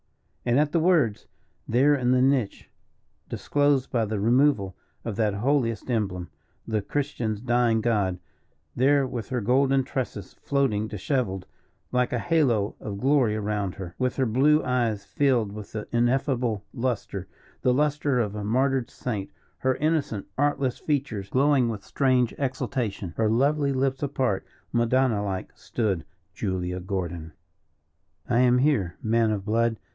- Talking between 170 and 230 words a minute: No, average, 145 wpm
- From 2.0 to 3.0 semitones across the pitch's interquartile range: No, average, 4.2 semitones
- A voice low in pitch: Yes, low, 120 Hz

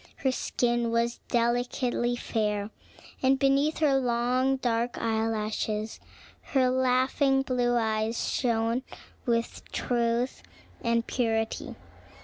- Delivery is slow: Yes, slow, 105 wpm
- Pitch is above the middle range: Yes, high, 240 Hz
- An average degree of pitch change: No, narrow, 2.1 semitones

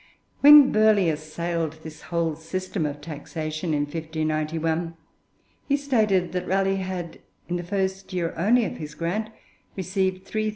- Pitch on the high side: No, medium, 175 Hz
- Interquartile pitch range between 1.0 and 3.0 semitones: No, average, 3.4 semitones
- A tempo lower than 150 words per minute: Yes, average, 140 wpm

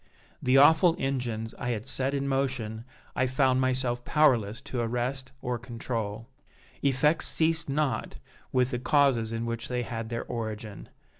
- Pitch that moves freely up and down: No, average, 2.7 semitones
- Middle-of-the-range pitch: No, low, 125 Hz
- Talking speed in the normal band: Yes, average, 150 wpm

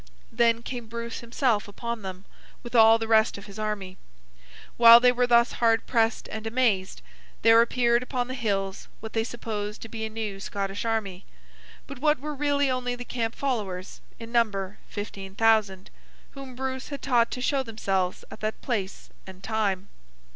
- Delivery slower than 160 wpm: No, average, 175 wpm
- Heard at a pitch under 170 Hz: No, high, 225 Hz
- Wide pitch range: No, average, 3.1 semitones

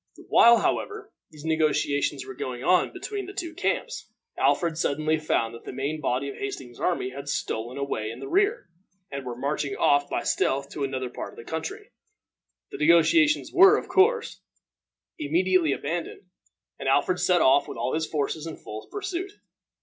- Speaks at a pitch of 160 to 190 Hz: No, medium, 150 Hz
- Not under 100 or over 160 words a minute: No, average, 175 wpm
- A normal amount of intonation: No, wide, 5.7 semitones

